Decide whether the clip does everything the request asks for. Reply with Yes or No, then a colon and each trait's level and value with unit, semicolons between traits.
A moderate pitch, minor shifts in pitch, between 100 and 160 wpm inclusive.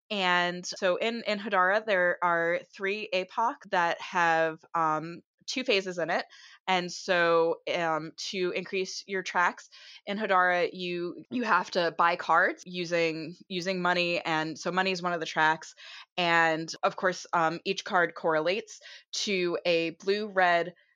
Yes: medium, 180 Hz; narrow, 2.1 semitones; average, 150 wpm